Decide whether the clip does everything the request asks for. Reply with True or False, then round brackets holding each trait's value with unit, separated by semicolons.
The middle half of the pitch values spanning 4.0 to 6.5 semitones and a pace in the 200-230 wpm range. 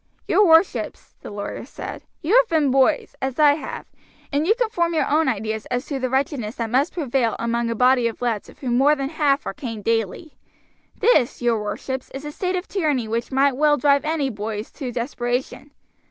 True (4.3 semitones; 205 wpm)